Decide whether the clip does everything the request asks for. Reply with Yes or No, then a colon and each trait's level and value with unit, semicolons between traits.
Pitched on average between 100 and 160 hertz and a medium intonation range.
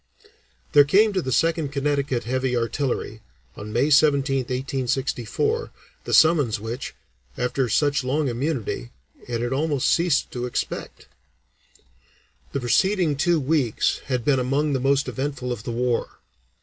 Yes: low, 135 Hz; average, 3.1 semitones